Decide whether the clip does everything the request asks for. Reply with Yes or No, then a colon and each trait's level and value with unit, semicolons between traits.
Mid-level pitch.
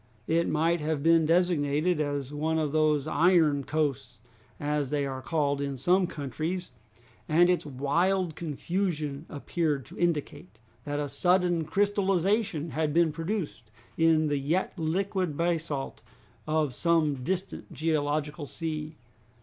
Yes: medium, 155 Hz